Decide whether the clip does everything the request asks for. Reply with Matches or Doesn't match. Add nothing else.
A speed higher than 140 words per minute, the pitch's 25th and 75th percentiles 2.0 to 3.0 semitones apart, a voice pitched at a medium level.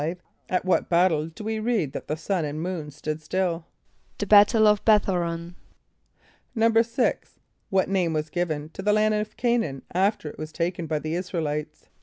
Doesn't match